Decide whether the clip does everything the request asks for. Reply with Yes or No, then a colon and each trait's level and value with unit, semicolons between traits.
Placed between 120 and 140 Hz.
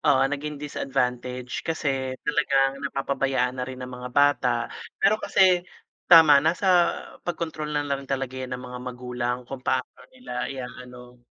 Yes: low, 135 Hz